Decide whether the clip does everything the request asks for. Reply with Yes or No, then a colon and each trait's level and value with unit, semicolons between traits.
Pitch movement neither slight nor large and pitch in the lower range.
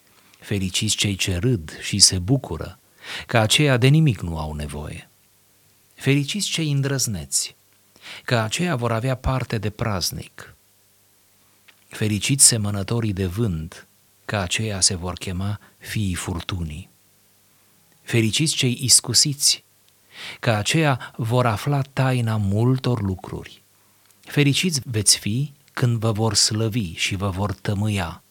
Yes: average, 4.2 semitones; low, 105 Hz